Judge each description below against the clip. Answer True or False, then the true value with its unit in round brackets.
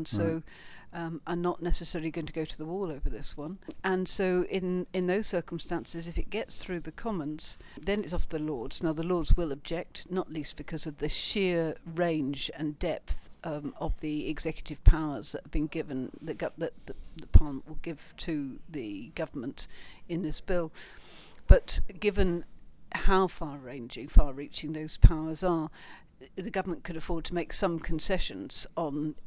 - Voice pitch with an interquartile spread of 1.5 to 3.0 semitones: True (2.6 semitones)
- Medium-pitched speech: True (165 Hz)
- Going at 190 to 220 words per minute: False (175 wpm)